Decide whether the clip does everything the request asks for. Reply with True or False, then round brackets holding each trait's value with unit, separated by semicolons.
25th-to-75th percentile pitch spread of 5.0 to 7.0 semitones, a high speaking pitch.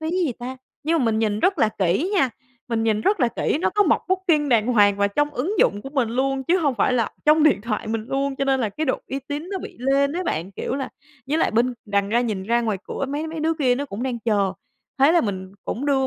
True (5.3 semitones; 260 Hz)